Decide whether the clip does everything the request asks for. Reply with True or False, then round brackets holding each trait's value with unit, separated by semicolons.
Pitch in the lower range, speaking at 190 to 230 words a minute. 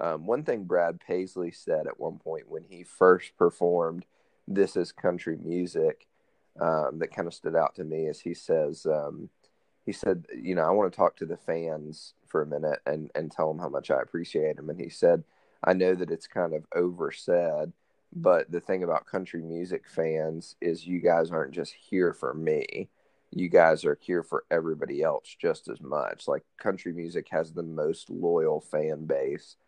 True (90 Hz; 195 wpm)